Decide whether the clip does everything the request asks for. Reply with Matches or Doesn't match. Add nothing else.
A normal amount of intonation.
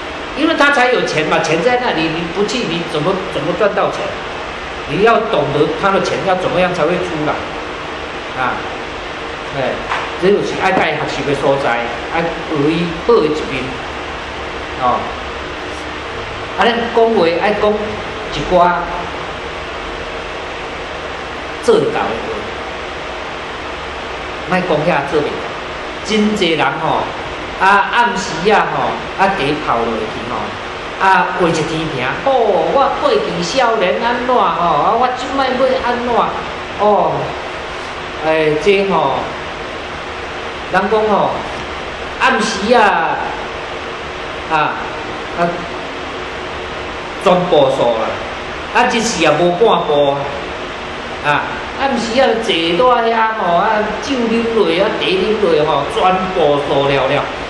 Doesn't match